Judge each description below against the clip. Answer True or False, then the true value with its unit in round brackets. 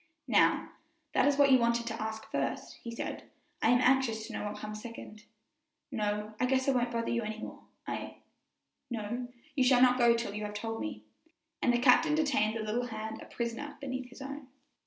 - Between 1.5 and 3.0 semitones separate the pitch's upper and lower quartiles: True (2.7 semitones)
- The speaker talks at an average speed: False (210 wpm)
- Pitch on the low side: False (235 Hz)